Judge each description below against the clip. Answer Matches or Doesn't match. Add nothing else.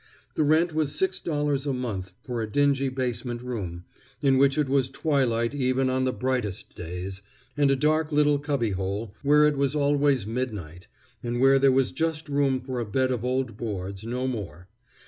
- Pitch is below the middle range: Matches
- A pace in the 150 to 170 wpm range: Doesn't match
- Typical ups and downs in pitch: Matches